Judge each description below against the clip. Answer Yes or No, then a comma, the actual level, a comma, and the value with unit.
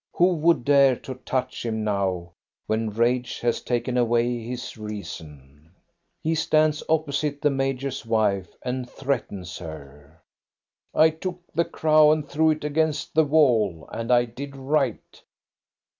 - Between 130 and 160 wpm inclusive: Yes, average, 145 wpm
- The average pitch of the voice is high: No, low, 125 Hz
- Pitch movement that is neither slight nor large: No, wide, 5.7 semitones